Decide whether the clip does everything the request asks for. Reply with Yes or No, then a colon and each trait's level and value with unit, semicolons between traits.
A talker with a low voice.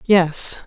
No: medium, 175 Hz